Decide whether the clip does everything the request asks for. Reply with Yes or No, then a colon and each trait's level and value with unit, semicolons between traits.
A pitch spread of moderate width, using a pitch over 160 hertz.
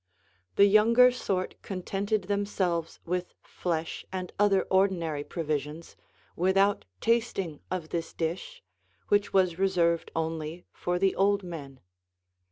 Yes: average, 3.3 semitones; medium, 185 Hz